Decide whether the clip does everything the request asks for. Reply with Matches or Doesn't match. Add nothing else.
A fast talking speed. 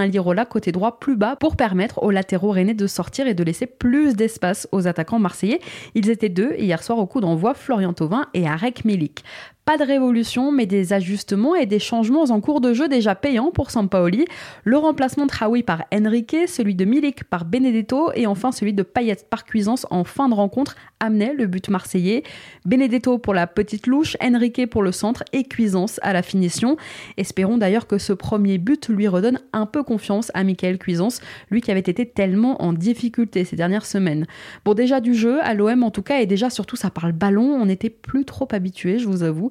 Doesn't match